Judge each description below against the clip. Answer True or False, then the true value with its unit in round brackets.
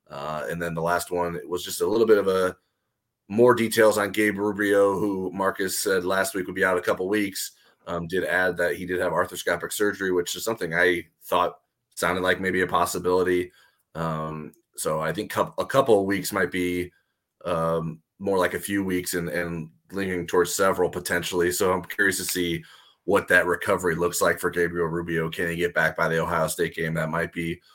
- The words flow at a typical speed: False (210 wpm)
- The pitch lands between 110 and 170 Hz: False (90 Hz)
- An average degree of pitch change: False (2.2 semitones)